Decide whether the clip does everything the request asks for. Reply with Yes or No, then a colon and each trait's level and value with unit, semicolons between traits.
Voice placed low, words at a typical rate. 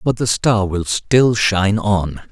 Yes: low, 105 Hz; average, 180 wpm